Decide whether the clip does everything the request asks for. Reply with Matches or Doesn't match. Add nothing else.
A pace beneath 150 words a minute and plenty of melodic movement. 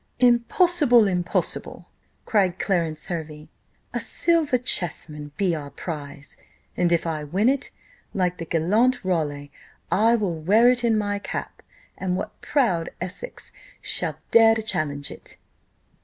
Matches